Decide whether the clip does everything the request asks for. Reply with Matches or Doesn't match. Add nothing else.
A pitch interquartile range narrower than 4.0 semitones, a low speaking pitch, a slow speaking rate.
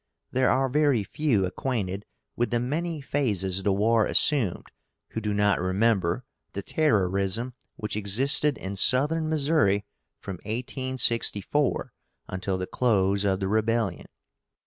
Doesn't match